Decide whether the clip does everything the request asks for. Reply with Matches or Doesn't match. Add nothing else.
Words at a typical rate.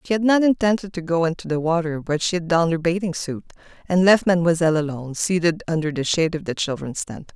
Doesn't match